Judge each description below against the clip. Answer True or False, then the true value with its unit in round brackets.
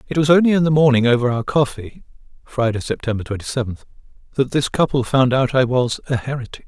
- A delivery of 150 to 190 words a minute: False (200 wpm)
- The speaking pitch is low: True (130 Hz)